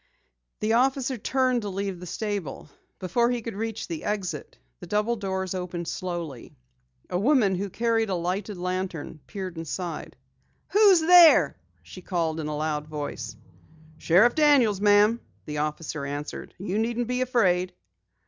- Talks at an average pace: Yes, average, 150 wpm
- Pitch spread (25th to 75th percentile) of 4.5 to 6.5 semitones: Yes, average, 5.3 semitones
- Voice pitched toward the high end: Yes, high, 195 Hz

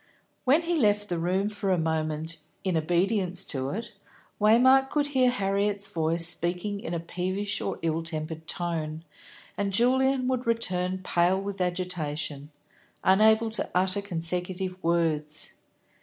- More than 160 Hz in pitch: Yes, medium, 185 Hz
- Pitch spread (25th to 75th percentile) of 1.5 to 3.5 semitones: No, average, 3.9 semitones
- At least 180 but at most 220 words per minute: No, average, 140 wpm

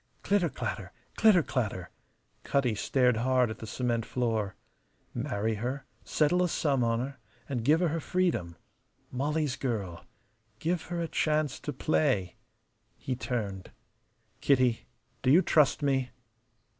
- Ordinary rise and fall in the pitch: Yes, average, 4.9 semitones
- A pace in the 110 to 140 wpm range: Yes, slow, 135 wpm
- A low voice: Yes, low, 130 Hz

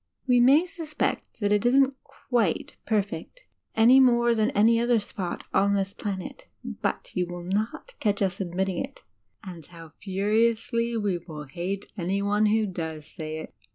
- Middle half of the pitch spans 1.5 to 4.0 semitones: No, average, 4.4 semitones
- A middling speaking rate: Yes, average, 155 wpm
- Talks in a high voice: Yes, high, 205 Hz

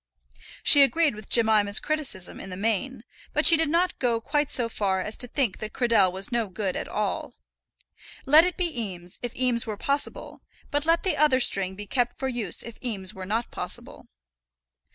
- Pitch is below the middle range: No, high, 235 Hz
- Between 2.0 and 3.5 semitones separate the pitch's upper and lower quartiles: No, wide, 5.6 semitones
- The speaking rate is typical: Yes, average, 195 wpm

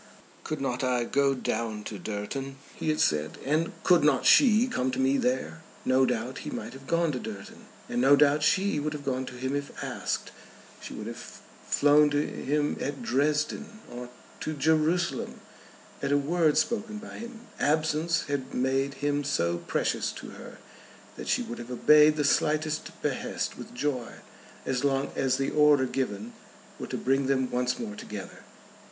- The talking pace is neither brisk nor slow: Yes, average, 175 wpm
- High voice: No, medium, 140 Hz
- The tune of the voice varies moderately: Yes, average, 3.2 semitones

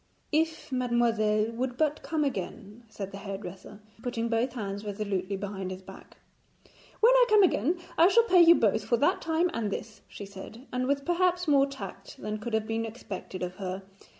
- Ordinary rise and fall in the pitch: No, wide, 6.5 semitones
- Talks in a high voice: Yes, high, 230 Hz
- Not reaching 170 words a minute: No, average, 180 wpm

